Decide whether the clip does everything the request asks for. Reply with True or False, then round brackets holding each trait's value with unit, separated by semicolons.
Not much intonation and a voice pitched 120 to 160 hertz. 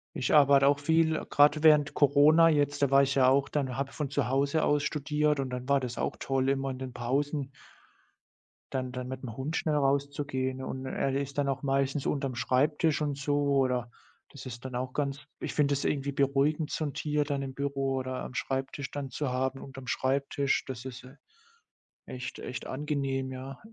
True (1.7 semitones; 135 Hz)